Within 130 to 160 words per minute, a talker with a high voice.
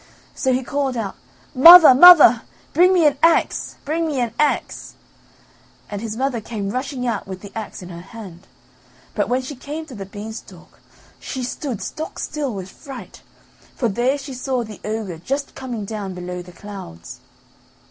No: average, 170 wpm; high, 245 Hz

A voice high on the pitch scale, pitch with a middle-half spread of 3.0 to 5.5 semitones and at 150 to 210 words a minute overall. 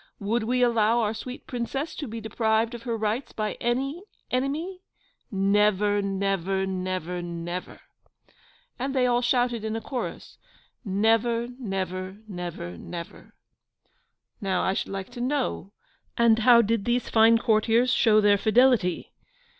No: high, 220 Hz; average, 3.7 semitones; average, 140 wpm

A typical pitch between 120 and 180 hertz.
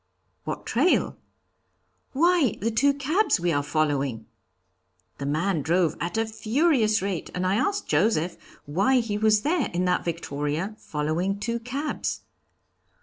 No: high, 200 Hz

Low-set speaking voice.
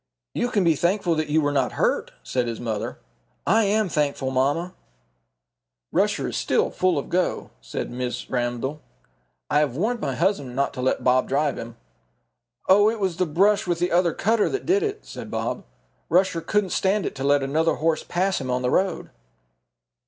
No: medium, 165 Hz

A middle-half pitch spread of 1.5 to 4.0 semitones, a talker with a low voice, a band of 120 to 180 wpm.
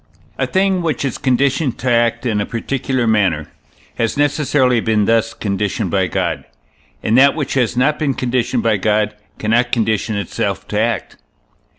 Yes: average, 3.7 semitones; low, 115 Hz; average, 165 wpm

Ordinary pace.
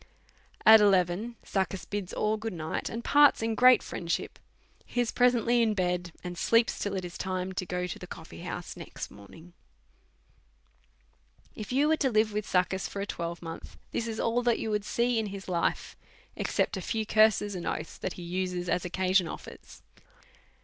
Yes: average, 185 wpm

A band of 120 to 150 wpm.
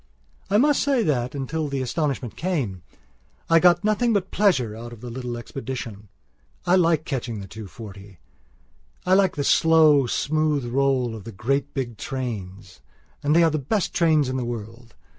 No: average, 170 wpm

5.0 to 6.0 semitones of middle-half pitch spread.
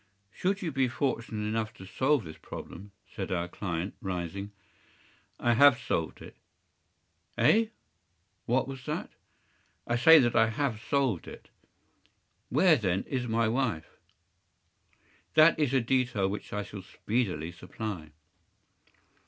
Yes: average, 5.3 semitones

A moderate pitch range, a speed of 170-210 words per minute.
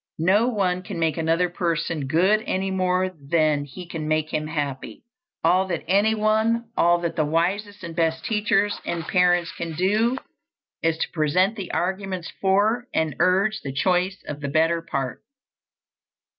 No: average, 3.5 semitones; average, 155 wpm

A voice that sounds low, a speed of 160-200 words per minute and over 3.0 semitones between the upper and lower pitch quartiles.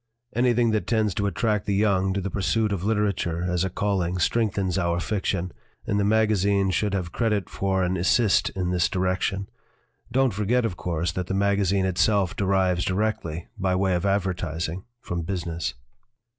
No: very low, 95 Hz; average, 170 wpm; narrow, 2.5 semitones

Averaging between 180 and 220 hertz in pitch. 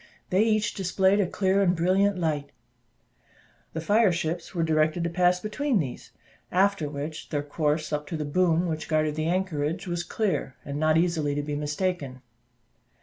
No: medium, 165 Hz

